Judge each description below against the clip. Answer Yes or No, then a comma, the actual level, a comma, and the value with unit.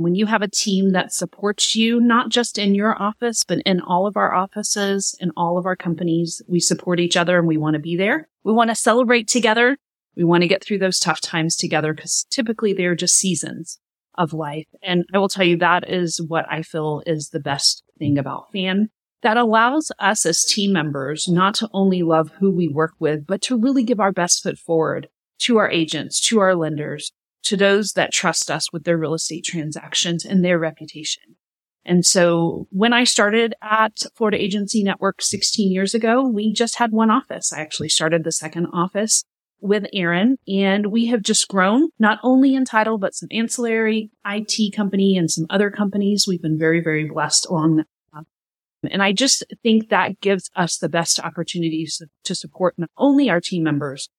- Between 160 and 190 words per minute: No, average, 200 wpm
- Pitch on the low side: No, medium, 185 Hz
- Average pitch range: Yes, average, 4.3 semitones